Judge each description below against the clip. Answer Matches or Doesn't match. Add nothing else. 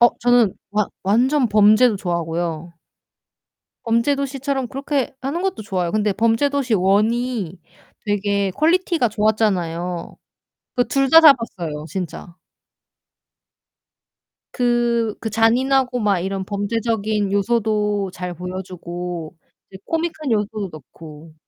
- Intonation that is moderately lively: Matches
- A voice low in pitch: Doesn't match